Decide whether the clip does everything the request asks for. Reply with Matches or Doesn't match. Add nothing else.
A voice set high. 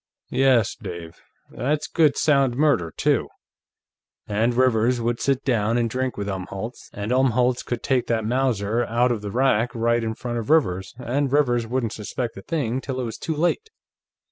Doesn't match